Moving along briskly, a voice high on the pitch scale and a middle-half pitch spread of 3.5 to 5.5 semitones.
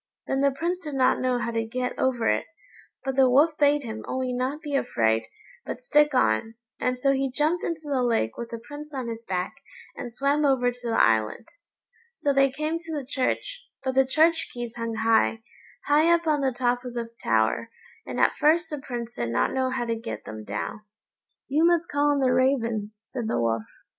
Yes: fast, 210 wpm; very high, 255 Hz; average, 4.1 semitones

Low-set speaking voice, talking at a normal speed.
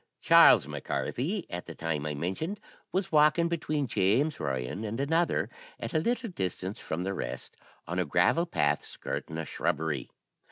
Yes: low, 100 Hz; average, 165 wpm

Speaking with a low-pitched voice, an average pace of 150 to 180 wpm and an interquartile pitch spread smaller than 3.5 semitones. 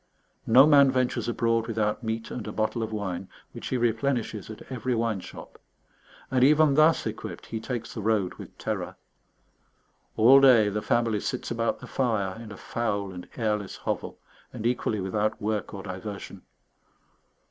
Yes: low, 115 Hz; average, 165 wpm; average, 2.9 semitones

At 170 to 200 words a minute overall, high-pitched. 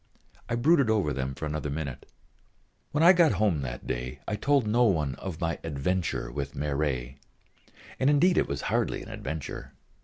No: average, 175 wpm; very low, 80 Hz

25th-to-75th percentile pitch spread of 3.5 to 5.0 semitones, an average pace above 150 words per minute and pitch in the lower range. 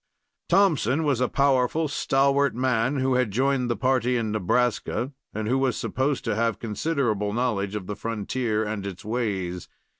Yes: average, 3.9 semitones; average, 160 wpm; low, 125 Hz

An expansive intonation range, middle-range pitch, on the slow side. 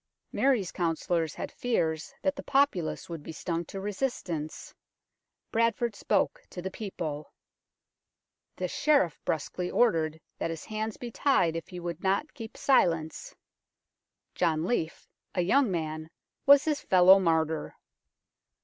Yes: wide, 6.5 semitones; medium, 180 Hz; slow, 130 wpm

